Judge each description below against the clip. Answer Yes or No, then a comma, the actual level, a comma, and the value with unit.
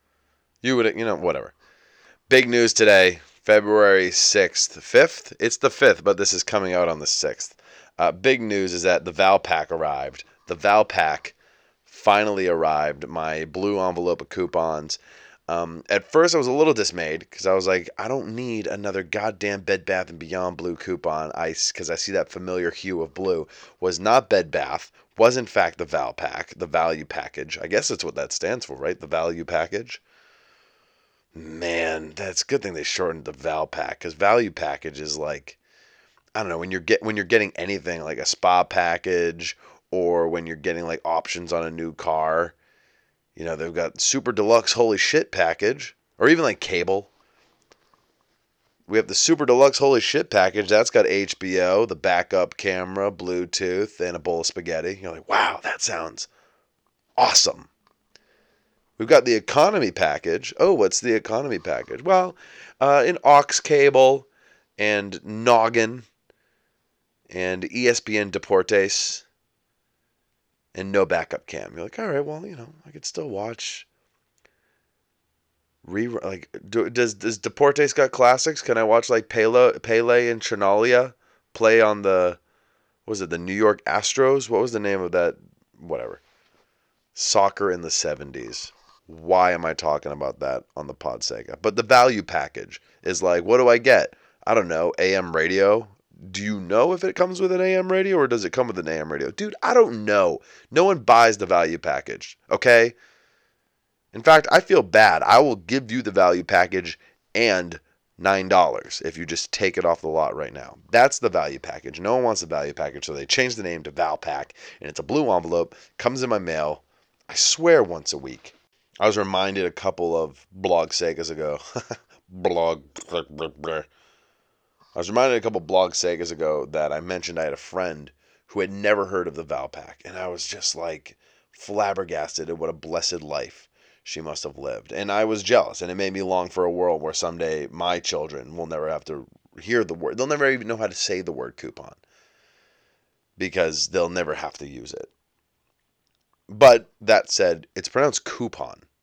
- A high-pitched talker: No, low, 100 Hz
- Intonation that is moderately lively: No, wide, 6.6 semitones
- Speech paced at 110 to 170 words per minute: No, average, 180 wpm